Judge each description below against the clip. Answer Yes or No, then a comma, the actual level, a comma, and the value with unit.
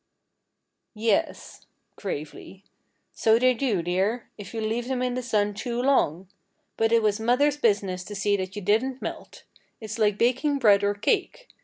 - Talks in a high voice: Yes, high, 220 Hz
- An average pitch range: Yes, average, 3.5 semitones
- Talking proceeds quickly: No, average, 165 wpm